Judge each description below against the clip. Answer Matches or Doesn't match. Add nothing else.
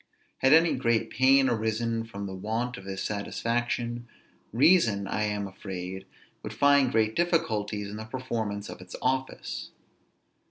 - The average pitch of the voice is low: Matches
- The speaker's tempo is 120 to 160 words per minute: Matches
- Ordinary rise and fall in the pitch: Matches